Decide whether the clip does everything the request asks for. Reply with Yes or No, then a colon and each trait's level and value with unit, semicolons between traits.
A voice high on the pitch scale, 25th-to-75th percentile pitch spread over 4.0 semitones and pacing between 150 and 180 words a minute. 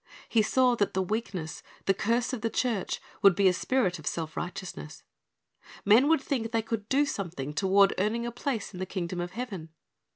No: high, 205 Hz; average, 4.5 semitones; average, 195 wpm